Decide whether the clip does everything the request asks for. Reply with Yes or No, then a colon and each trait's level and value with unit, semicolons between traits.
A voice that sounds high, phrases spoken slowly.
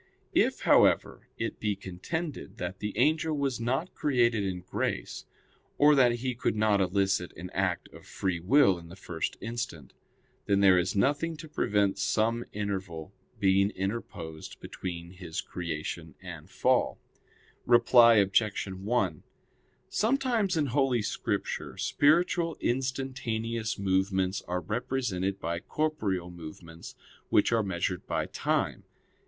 No: low, 100 Hz; slow, 130 wpm